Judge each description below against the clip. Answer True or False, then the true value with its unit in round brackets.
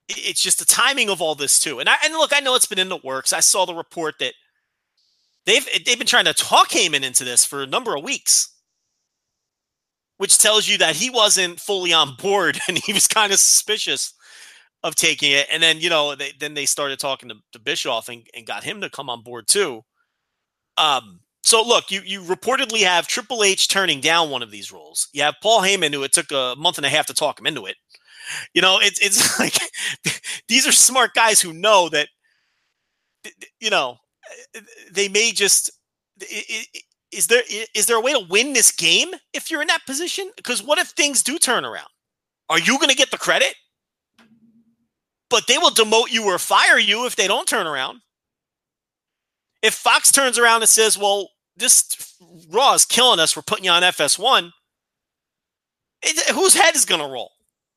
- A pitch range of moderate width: False (7.1 semitones)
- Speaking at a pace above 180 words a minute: True (200 wpm)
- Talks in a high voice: True (205 Hz)